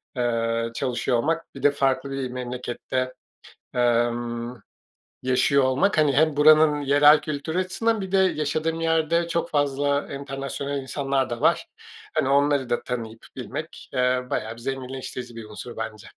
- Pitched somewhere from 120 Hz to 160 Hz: Yes, low, 135 Hz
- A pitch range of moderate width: Yes, average, 3.3 semitones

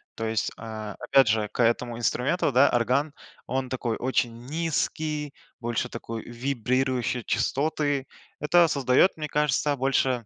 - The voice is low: Yes, low, 130 Hz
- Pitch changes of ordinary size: Yes, average, 3.5 semitones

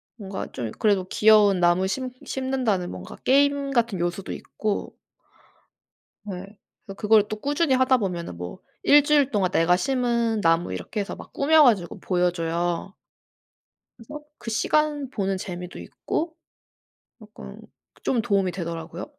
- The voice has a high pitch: Yes, high, 205 Hz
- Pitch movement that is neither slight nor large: No, wide, 6.5 semitones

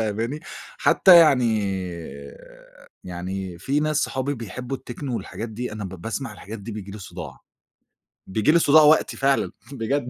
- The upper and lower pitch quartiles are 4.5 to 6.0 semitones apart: Yes, average, 5.2 semitones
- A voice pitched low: Yes, low, 115 Hz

